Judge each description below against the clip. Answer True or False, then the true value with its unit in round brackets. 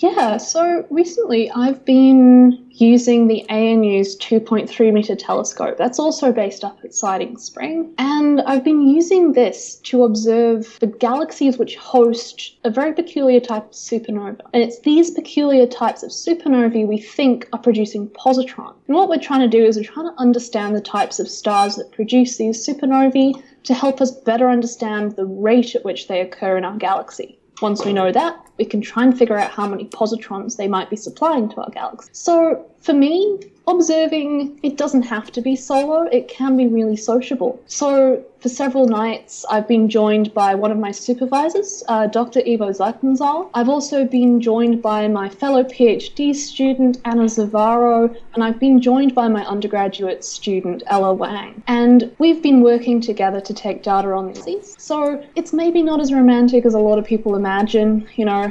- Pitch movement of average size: True (4.1 semitones)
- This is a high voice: True (240 Hz)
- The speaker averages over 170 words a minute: True (185 wpm)